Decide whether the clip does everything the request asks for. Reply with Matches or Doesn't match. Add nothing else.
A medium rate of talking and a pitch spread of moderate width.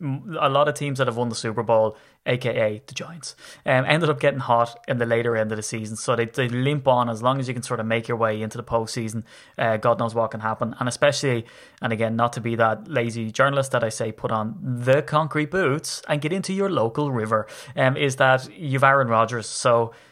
Doesn't match